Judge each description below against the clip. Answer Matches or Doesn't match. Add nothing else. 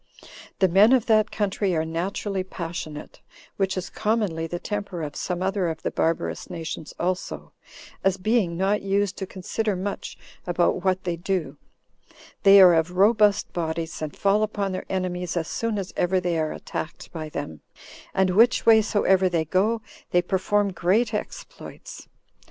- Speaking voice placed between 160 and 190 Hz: Matches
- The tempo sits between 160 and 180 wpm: Matches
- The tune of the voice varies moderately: Matches